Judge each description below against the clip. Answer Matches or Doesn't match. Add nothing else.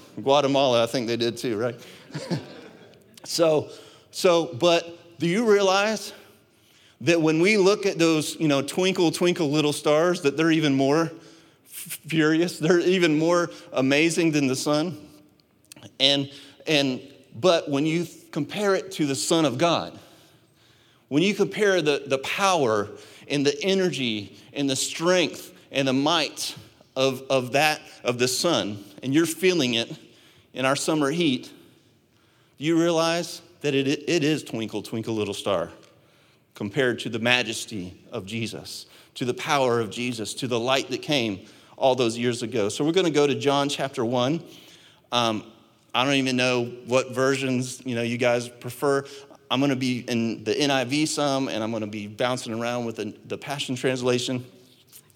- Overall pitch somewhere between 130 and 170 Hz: Matches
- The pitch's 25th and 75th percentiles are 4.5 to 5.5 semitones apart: Matches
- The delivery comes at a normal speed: Matches